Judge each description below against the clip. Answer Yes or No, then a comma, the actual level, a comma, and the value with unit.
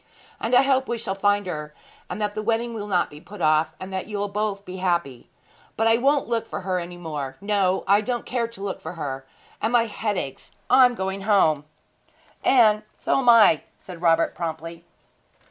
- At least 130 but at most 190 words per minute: No, fast, 205 wpm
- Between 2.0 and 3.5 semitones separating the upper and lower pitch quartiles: No, average, 4.9 semitones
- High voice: Yes, high, 200 Hz